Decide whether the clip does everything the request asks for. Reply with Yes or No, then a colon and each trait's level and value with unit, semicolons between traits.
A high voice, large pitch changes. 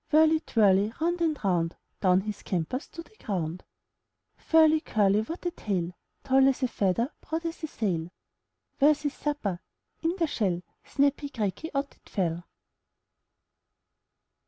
Yes: very high, 255 Hz; wide, 8.5 semitones